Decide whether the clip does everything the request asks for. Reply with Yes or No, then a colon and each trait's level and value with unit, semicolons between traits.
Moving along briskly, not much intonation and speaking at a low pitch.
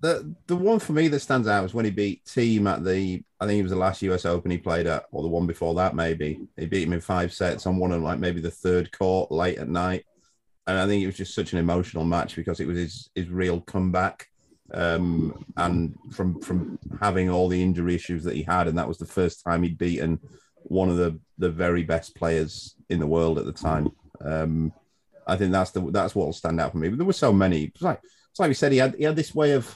Yes: fast, 260 wpm; narrow, 2.3 semitones; very low, 90 Hz